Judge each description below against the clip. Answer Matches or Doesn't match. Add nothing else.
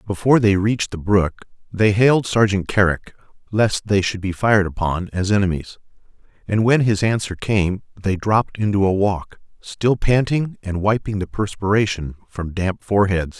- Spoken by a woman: Doesn't match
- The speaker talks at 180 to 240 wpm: Doesn't match